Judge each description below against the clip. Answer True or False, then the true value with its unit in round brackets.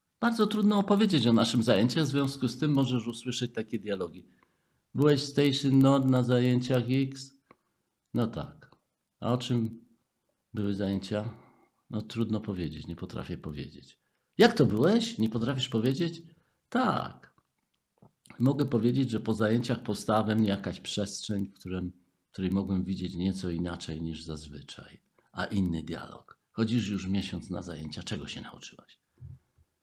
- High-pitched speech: False (115 Hz)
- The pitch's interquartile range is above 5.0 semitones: True (5.6 semitones)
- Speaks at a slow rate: False (140 wpm)